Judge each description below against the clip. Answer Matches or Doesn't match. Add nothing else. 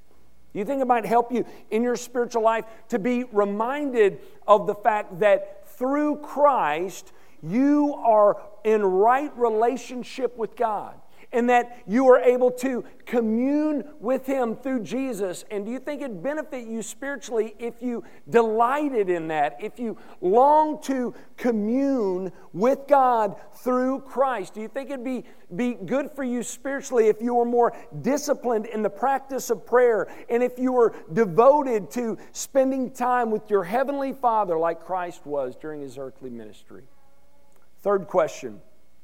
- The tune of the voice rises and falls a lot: Doesn't match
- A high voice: Matches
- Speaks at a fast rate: Doesn't match